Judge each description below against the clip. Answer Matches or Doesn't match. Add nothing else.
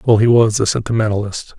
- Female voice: Doesn't match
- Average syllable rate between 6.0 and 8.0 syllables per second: Matches